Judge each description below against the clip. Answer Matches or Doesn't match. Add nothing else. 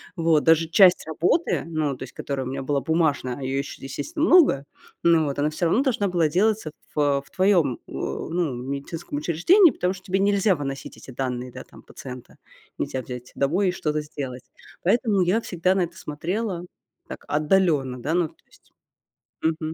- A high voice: Doesn't match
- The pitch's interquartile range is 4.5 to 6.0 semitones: Matches